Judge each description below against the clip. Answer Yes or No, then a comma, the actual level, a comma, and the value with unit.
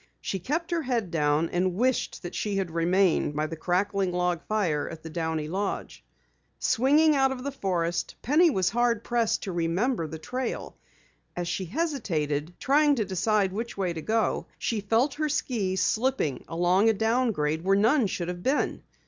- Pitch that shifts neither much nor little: No, wide, 6.2 semitones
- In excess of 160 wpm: Yes, average, 175 wpm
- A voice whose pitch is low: No, high, 195 Hz